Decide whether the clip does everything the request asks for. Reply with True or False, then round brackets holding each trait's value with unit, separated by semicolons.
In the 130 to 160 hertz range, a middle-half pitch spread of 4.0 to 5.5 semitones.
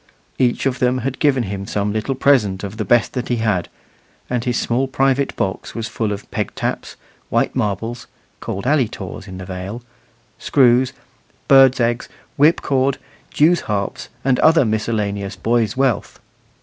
False (120 Hz; 4.4 semitones)